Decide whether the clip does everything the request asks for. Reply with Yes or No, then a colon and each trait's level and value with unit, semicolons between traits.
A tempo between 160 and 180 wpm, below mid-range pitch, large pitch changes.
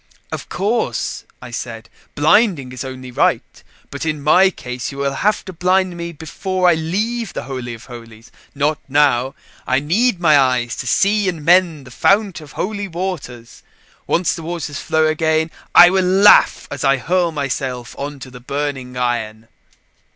No: average, 165 wpm; medium, 155 Hz; wide, 5.9 semitones